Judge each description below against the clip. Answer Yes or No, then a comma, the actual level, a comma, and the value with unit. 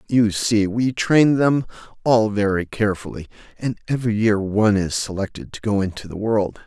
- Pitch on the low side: Yes, low, 105 Hz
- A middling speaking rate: Yes, average, 170 wpm